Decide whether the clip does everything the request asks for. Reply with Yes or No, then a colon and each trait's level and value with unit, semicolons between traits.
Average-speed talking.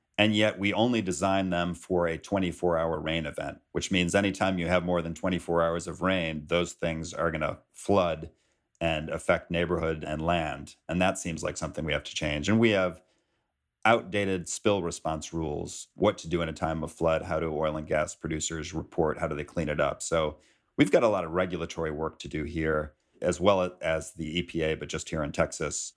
No: fast, 215 wpm